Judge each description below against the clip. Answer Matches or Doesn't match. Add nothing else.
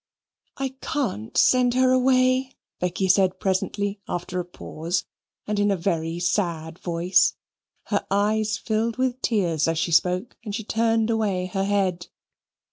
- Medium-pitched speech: Doesn't match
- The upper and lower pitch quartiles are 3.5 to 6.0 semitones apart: Matches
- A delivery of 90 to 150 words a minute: Matches